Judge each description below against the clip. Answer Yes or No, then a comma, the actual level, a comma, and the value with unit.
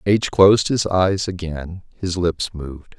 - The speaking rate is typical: Yes, average, 160 wpm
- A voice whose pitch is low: Yes, very low, 90 Hz